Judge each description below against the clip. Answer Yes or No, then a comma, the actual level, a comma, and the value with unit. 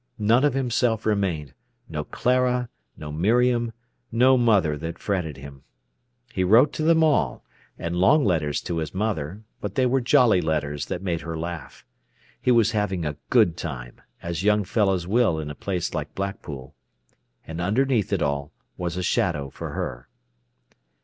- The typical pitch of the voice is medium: No, very low, 95 Hz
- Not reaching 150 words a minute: No, average, 160 wpm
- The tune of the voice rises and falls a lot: Yes, wide, 6.8 semitones